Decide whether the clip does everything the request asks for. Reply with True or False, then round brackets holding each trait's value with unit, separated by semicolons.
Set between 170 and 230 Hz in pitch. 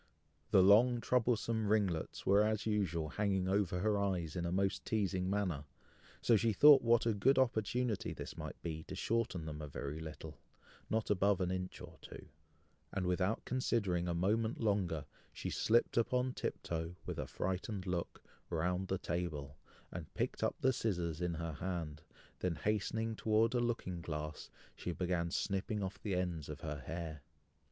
False (95 Hz)